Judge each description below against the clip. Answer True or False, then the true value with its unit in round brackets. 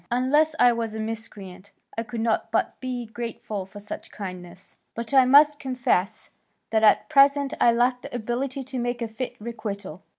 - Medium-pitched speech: False (235 Hz)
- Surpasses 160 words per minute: True (175 wpm)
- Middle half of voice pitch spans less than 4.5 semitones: True (3.1 semitones)